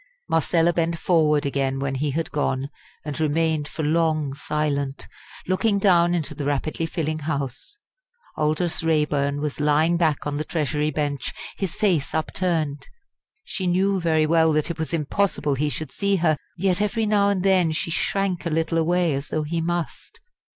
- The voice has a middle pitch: Yes, medium, 160 Hz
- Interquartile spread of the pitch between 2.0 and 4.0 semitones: Yes, average, 2.7 semitones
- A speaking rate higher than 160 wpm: Yes, average, 170 wpm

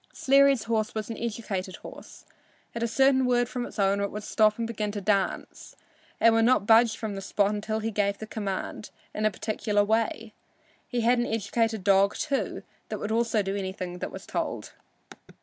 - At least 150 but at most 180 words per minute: No, average, 190 wpm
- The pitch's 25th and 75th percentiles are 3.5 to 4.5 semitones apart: No, narrow, 2.4 semitones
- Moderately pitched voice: No, high, 220 Hz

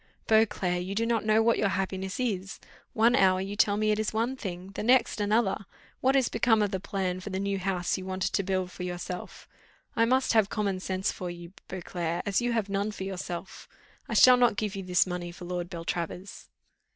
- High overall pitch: Yes, high, 195 Hz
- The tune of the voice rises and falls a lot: No, average, 3.0 semitones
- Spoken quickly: Yes, fast, 215 wpm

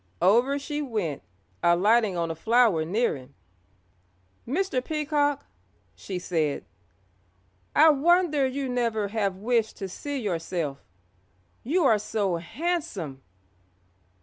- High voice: Yes, high, 225 Hz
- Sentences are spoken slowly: Yes, slow, 110 wpm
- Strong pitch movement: Yes, wide, 7.9 semitones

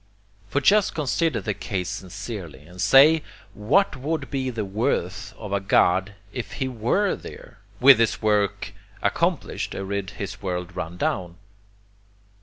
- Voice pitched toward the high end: No, low, 105 Hz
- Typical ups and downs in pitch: No, wide, 5.8 semitones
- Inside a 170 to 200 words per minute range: No, average, 145 wpm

